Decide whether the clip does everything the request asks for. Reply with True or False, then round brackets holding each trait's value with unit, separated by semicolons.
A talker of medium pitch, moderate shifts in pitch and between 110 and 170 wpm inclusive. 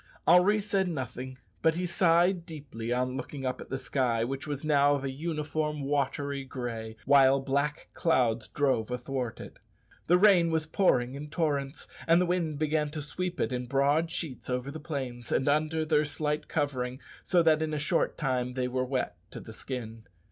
False (145 Hz; 3.6 semitones; 185 wpm)